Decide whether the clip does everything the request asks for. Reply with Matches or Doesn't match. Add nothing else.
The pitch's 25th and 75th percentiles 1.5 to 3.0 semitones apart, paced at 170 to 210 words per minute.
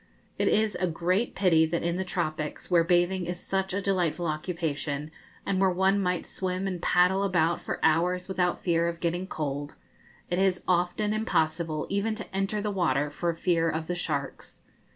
Matches